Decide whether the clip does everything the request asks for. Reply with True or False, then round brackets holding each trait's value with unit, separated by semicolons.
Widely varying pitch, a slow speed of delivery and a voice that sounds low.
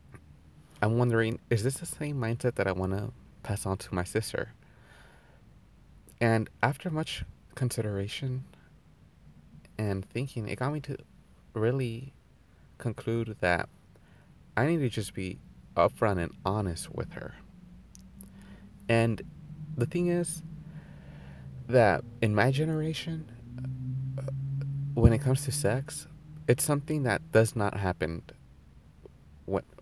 True (5.9 semitones; 120 wpm; 115 Hz)